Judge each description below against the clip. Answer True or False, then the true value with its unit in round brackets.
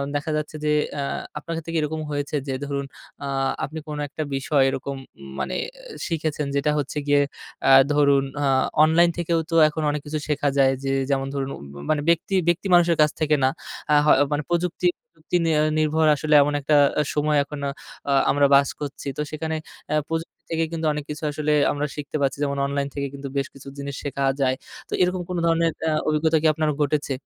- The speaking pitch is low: False (150 Hz)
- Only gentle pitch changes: True (2.1 semitones)